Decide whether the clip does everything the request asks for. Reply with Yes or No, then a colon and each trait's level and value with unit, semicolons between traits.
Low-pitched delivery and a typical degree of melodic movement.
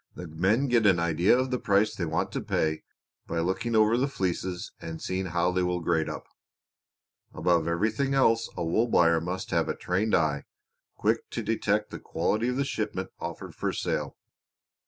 Yes: very low, 95 Hz; average, 4.9 semitones